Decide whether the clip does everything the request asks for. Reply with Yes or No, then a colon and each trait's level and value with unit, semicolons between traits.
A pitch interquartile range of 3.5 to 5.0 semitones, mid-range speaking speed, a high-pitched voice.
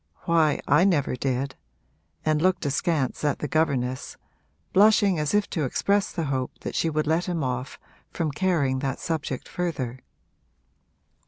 No: average, 4.4 semitones; average, 150 wpm; medium, 150 Hz